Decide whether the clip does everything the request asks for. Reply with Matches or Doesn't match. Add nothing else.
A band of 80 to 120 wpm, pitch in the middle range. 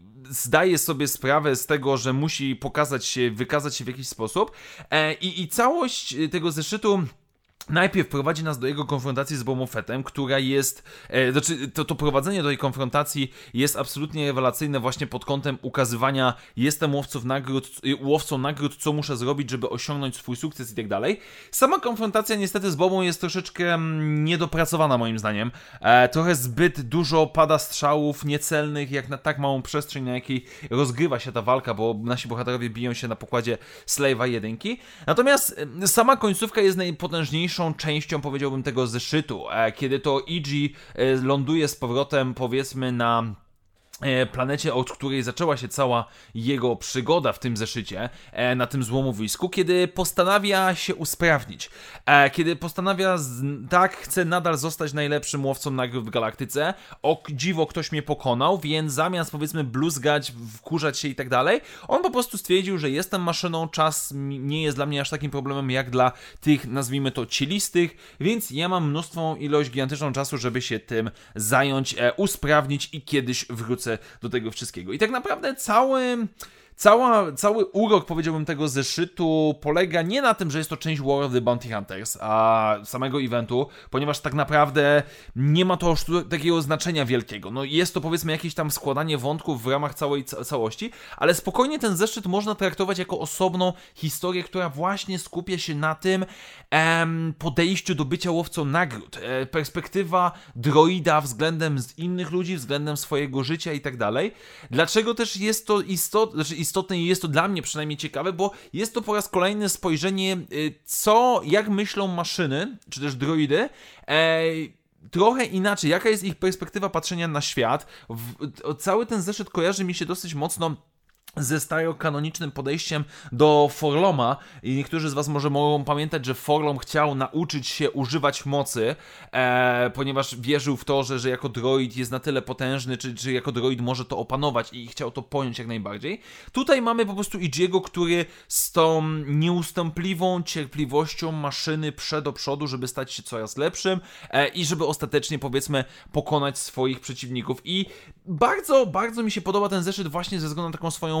Doesn't match